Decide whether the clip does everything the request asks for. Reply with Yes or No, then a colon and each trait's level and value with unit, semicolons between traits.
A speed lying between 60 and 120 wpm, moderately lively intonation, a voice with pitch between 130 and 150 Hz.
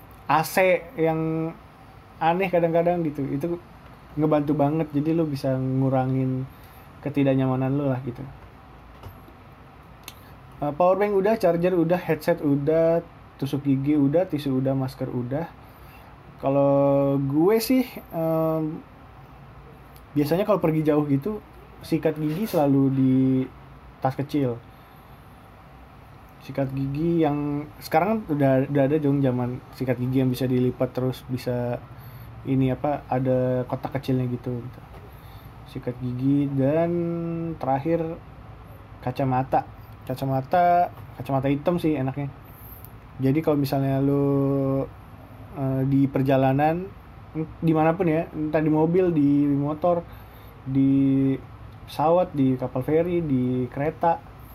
Yes: average, 110 wpm; average, 3.6 semitones; low, 135 Hz